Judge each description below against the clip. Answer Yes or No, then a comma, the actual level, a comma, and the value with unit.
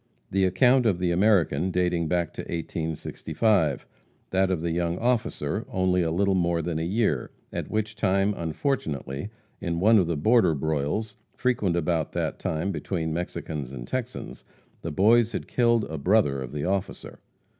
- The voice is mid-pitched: No, very low, 90 Hz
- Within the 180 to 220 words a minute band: No, average, 165 wpm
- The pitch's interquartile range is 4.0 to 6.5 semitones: Yes, average, 4.5 semitones